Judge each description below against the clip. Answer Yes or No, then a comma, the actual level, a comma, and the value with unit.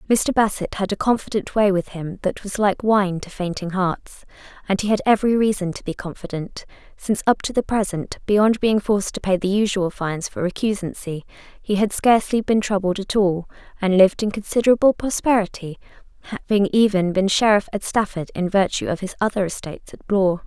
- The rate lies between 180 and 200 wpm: Yes, average, 190 wpm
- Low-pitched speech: No, high, 200 Hz